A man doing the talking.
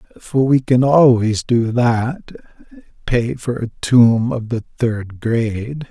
Yes: male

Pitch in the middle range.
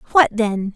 No: high, 225 Hz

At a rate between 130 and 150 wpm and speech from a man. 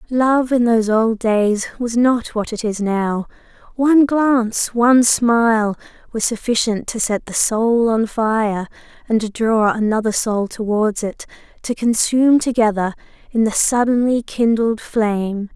No: average, 140 wpm; female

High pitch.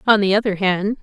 Yes: high, 200 Hz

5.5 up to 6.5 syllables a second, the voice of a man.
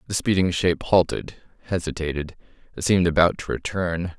Yes: 5.6 syllables/s; male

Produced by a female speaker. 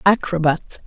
Yes: female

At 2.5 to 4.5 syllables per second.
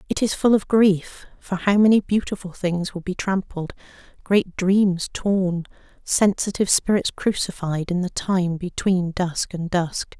Yes: 4.1 syllables/s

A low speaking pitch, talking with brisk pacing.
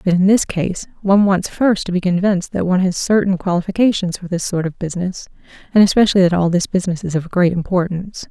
No: medium, 185 Hz; fast, 215 wpm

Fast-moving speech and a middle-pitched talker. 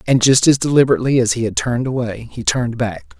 No: fast, 225 wpm; low, 120 Hz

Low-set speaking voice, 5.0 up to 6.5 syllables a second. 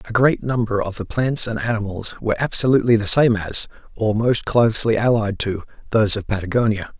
Yes: low, 110 Hz; 5.8 syllables/s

